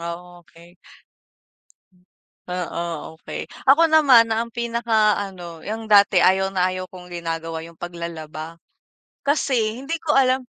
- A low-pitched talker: No, high, 190 Hz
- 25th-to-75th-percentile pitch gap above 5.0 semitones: Yes, wide, 5.5 semitones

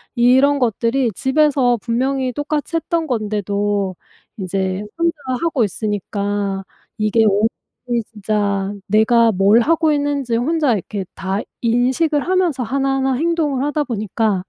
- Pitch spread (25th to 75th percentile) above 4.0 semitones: Yes, wide, 5.5 semitones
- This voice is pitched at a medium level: No, high, 240 Hz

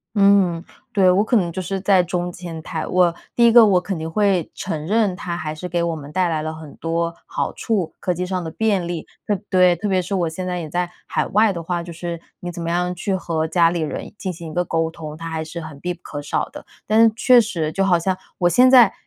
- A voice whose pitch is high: No, medium, 175 Hz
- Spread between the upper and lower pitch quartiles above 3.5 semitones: No, narrow, 2.6 semitones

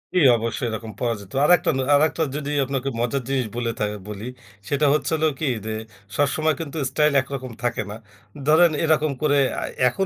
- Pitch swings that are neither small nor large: Yes, average, 4.2 semitones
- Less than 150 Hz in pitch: Yes, medium, 140 Hz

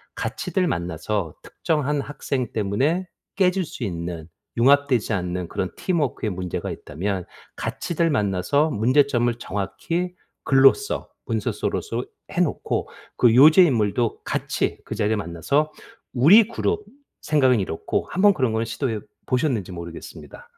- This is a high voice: No, low, 125 Hz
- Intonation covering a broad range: Yes, wide, 7.5 semitones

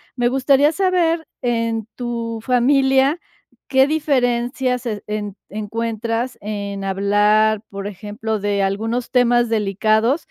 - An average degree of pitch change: Yes, average, 3.5 semitones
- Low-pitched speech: No, high, 230 Hz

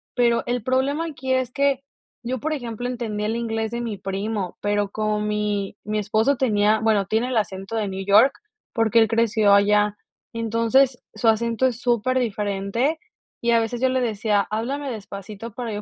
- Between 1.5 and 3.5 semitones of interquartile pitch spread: Yes, average, 2.9 semitones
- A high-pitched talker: Yes, high, 225 Hz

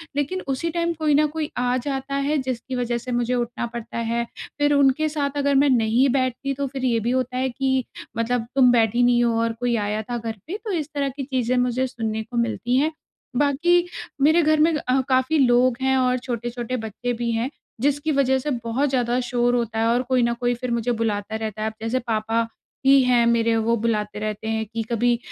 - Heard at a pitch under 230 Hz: No, high, 245 Hz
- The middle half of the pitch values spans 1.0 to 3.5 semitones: Yes, average, 2.8 semitones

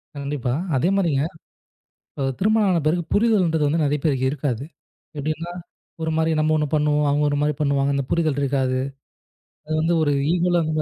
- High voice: No, medium, 150 Hz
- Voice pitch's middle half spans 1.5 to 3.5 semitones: Yes, average, 2.9 semitones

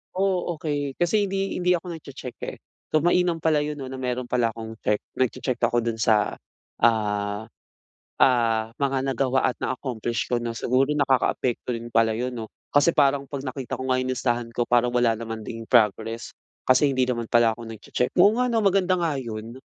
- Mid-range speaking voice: No, low, 125 Hz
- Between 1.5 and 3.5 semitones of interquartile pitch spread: No, average, 4.0 semitones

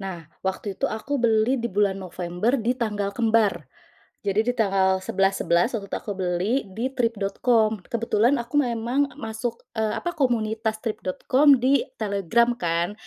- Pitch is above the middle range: Yes, high, 220 Hz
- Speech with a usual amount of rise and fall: Yes, average, 3.7 semitones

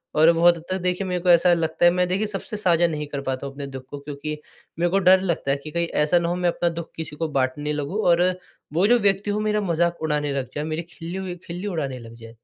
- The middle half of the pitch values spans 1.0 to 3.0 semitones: No, average, 3.4 semitones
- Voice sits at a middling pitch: Yes, medium, 170 Hz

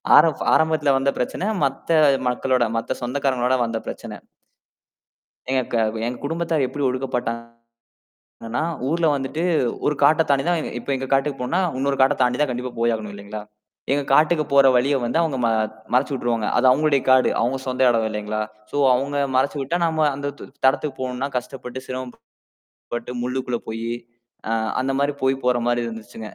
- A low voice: Yes, low, 130 Hz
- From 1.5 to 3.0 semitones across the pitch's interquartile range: Yes, average, 2.7 semitones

